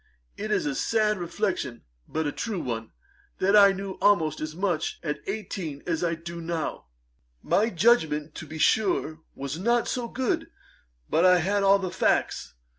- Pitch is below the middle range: No, medium, 185 Hz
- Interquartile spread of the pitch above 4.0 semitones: Yes, average, 4.9 semitones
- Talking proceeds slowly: No, average, 170 wpm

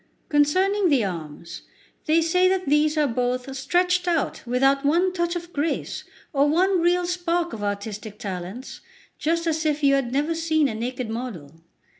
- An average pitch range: No, wide, 5.8 semitones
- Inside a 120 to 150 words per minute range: No, average, 165 wpm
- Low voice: No, very high, 295 Hz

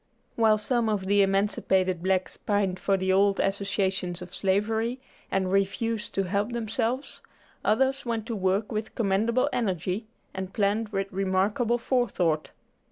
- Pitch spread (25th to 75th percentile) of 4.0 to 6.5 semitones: No, average, 2.9 semitones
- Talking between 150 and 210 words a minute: No, average, 140 wpm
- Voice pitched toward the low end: No, high, 200 Hz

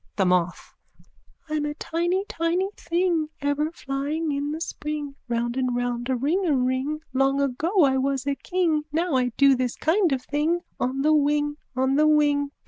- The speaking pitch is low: No, very high, 290 Hz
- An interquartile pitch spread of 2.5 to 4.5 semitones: Yes, average, 3.2 semitones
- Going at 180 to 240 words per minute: No, average, 170 wpm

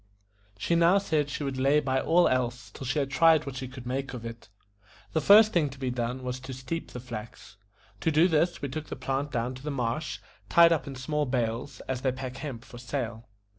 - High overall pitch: No, low, 135 Hz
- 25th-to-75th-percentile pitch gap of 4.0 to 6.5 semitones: No, average, 3.2 semitones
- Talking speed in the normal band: No, fast, 230 wpm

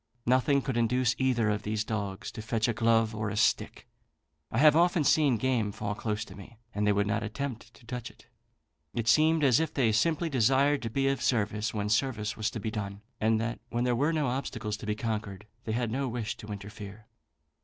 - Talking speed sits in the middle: No, fast, 220 wpm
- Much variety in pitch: No, average, 3.5 semitones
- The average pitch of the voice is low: Yes, low, 115 Hz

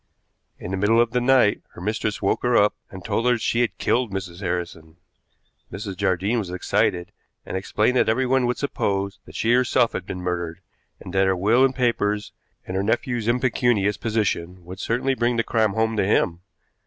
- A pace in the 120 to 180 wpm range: No, average, 195 wpm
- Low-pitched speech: Yes, low, 105 Hz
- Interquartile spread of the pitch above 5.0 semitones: No, average, 4.3 semitones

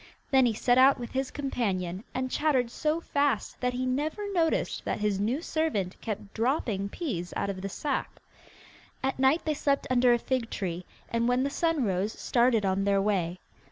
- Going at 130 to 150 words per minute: No, average, 190 wpm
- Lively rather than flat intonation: Yes, wide, 5.7 semitones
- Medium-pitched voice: No, high, 245 Hz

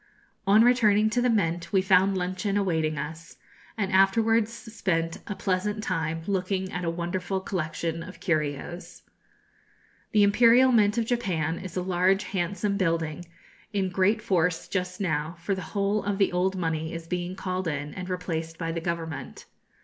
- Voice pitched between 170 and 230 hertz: Yes, medium, 185 Hz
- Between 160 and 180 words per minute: Yes, average, 165 wpm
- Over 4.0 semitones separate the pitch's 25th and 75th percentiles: No, average, 3.4 semitones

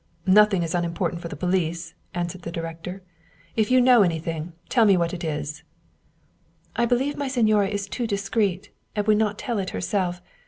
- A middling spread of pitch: Yes, average, 4.1 semitones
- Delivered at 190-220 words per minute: Yes, average, 195 wpm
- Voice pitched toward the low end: No, high, 190 Hz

